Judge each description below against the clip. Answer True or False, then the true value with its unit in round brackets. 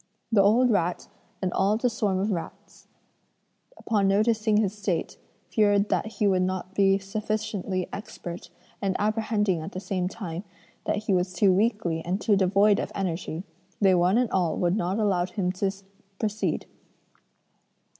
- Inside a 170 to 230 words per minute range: False (155 wpm)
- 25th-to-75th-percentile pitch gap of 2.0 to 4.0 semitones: True (2.5 semitones)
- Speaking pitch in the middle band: False (195 Hz)